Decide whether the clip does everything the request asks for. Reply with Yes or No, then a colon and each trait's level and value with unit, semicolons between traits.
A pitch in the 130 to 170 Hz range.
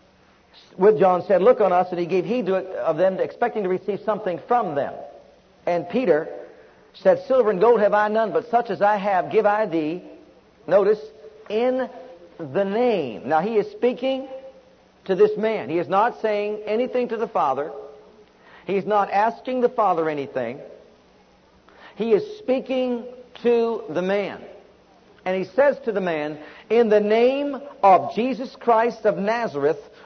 No: high, 215 Hz